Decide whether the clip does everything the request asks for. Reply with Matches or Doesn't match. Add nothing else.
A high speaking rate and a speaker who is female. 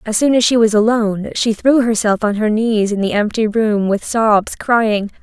Matches